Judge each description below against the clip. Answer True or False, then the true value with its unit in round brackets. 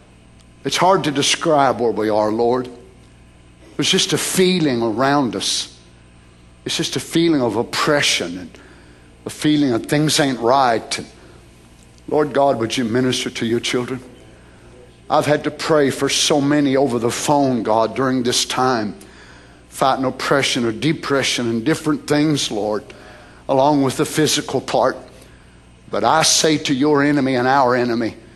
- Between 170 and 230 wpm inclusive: False (150 wpm)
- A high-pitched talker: False (125 Hz)